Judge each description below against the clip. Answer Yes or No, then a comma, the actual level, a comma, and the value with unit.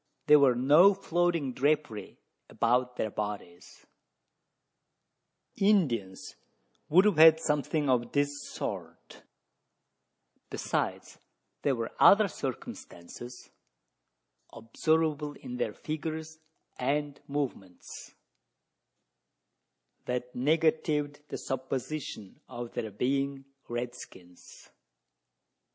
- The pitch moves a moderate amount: Yes, average, 4.2 semitones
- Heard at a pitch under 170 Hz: Yes, medium, 140 Hz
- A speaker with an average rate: No, slow, 85 wpm